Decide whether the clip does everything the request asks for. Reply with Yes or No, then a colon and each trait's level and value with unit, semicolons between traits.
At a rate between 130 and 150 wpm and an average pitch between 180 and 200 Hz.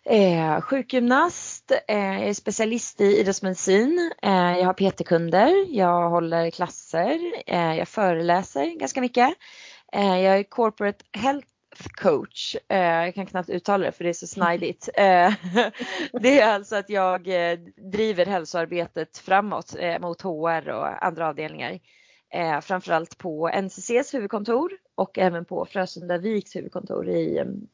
Yes: average, 140 wpm; high, 190 Hz